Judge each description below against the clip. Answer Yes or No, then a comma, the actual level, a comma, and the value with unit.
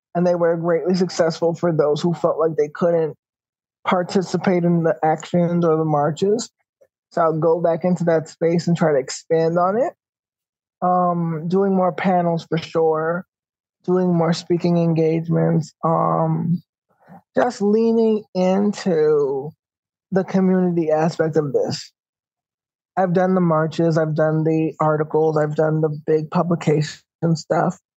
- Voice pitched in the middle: Yes, medium, 170 Hz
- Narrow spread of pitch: Yes, narrow, 2.2 semitones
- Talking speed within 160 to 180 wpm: No, average, 140 wpm